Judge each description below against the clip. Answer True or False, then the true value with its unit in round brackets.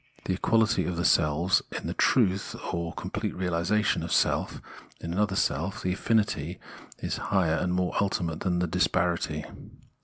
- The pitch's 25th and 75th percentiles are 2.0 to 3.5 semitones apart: True (2.7 semitones)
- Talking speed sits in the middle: True (155 wpm)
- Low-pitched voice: True (90 Hz)